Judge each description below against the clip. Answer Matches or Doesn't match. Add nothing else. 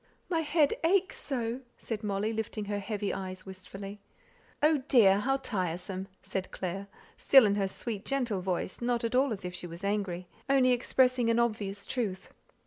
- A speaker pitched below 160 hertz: Doesn't match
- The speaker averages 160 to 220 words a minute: Matches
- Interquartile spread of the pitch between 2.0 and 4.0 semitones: Doesn't match